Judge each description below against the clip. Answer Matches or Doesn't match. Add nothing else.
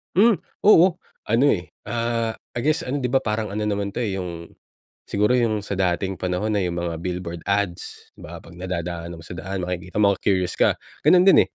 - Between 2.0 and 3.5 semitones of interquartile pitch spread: Doesn't match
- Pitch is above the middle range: Doesn't match